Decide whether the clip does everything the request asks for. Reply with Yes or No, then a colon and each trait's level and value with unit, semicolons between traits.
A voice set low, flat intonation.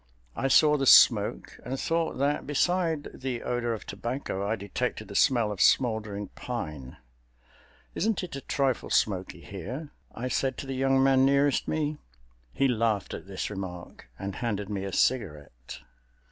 No: low, 120 Hz; wide, 5.5 semitones